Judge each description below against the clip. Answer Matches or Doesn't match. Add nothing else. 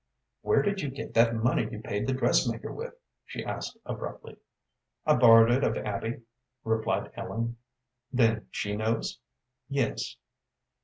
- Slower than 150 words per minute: Matches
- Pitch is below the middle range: Matches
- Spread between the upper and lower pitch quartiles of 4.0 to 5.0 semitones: Doesn't match